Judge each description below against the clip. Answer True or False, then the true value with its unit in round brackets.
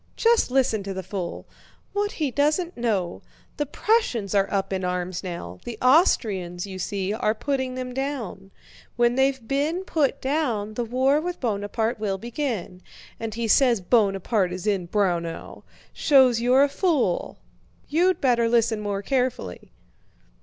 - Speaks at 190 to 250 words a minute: False (150 wpm)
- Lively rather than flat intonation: True (5.8 semitones)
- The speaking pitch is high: True (230 Hz)